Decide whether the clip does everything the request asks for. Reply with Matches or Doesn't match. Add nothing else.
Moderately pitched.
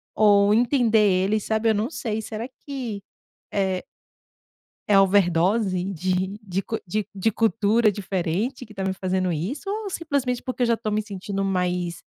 Doesn't match